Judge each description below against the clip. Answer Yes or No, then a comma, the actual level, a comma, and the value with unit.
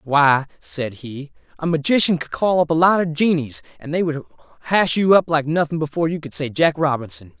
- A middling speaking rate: No, fast, 210 wpm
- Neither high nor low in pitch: Yes, medium, 155 Hz